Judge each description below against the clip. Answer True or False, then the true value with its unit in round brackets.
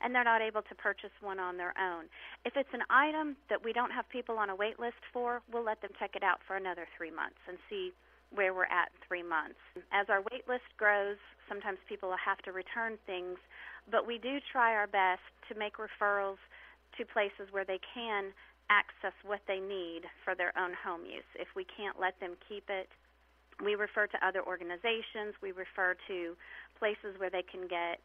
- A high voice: True (200 Hz)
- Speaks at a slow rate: False (205 wpm)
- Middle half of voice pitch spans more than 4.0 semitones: False (3.3 semitones)